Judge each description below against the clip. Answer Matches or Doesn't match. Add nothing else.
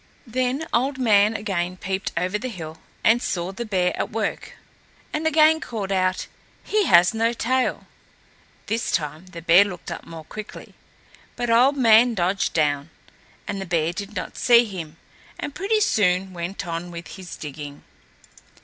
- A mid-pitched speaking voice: Doesn't match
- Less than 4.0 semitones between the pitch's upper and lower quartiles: Doesn't match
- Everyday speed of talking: Matches